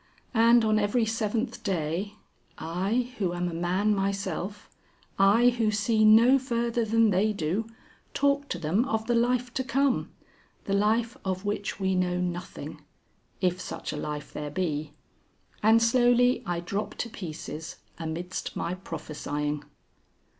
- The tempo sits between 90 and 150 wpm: Yes, average, 145 wpm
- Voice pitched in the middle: No, high, 205 Hz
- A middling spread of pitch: Yes, average, 4.7 semitones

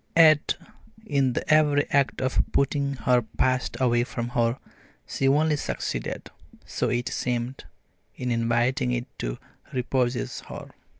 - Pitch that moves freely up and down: No, narrow, 2.4 semitones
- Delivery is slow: Yes, slow, 130 wpm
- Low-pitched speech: Yes, low, 130 Hz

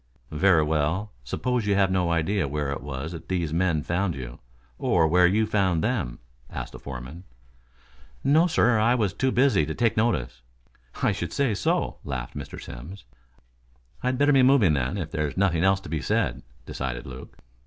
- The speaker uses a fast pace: No, average, 180 wpm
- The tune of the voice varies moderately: No, wide, 6.2 semitones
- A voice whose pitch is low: Yes, very low, 90 Hz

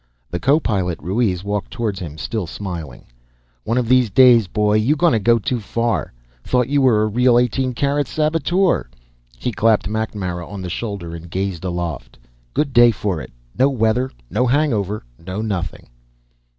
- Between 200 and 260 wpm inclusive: No, average, 165 wpm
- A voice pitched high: No, low, 110 Hz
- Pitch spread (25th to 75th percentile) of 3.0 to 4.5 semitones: No, average, 5.1 semitones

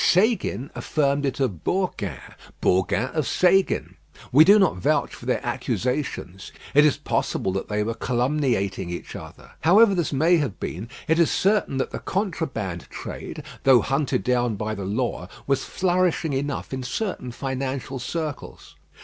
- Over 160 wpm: No, average, 155 wpm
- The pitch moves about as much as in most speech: No, wide, 6.0 semitones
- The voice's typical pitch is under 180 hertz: Yes, low, 135 Hz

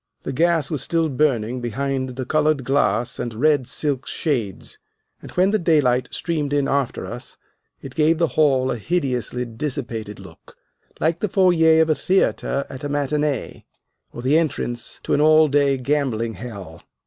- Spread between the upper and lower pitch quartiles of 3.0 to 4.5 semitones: Yes, average, 4.0 semitones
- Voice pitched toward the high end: No, medium, 140 Hz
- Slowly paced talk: No, average, 165 wpm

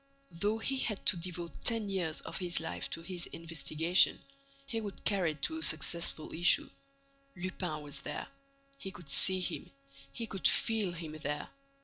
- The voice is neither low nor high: Yes, medium, 175 Hz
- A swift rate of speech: No, average, 165 wpm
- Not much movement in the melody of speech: No, average, 3.3 semitones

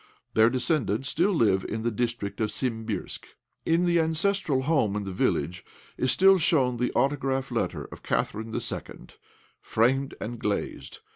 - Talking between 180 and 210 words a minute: No, average, 155 wpm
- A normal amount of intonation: No, wide, 5.8 semitones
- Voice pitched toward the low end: Yes, low, 125 Hz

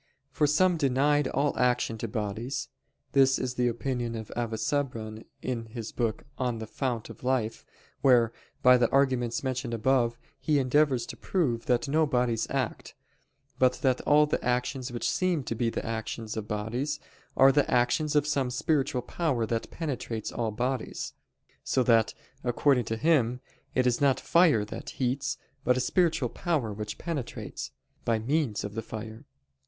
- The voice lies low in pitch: Yes, low, 125 Hz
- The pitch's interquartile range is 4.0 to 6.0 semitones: No, average, 3.4 semitones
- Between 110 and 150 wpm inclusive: No, average, 165 wpm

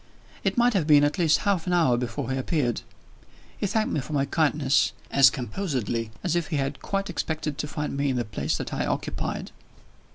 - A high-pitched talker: No, medium, 150 Hz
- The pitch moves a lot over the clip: No, average, 4.5 semitones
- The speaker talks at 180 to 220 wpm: Yes, fast, 205 wpm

